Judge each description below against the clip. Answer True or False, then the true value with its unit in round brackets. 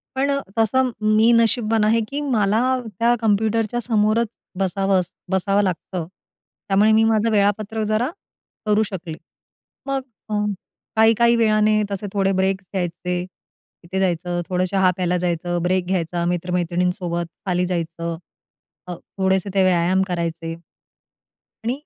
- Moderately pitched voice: False (195 Hz)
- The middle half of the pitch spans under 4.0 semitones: True (3.5 semitones)